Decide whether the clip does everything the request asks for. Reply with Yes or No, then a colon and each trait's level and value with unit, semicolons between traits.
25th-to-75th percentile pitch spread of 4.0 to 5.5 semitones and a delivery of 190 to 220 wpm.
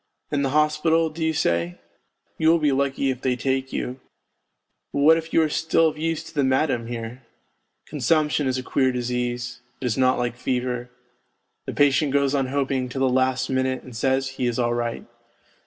No: average, 2.9 semitones; average, 195 wpm